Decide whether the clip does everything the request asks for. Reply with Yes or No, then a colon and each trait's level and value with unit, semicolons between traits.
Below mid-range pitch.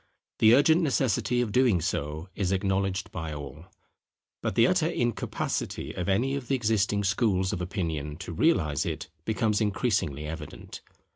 Yes: low, 100 Hz